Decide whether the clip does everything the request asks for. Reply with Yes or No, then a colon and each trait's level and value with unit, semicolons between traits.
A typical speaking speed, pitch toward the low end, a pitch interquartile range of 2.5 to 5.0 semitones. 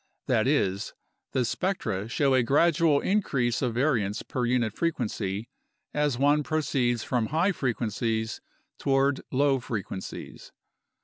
No: slow, 130 wpm; low, 130 Hz; average, 4.3 semitones